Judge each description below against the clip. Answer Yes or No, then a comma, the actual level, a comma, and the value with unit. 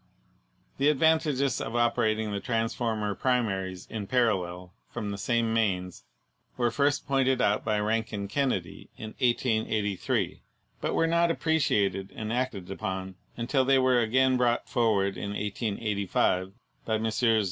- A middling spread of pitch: Yes, average, 4.1 semitones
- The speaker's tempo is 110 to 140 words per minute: Yes, slow, 135 wpm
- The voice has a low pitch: Yes, low, 110 Hz